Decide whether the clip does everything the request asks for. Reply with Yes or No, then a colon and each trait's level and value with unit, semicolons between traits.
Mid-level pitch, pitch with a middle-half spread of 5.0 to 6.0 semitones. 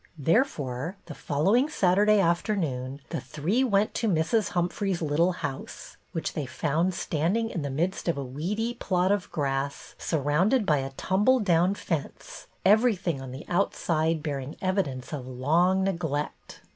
Yes: medium, 170 Hz; average, 5.3 semitones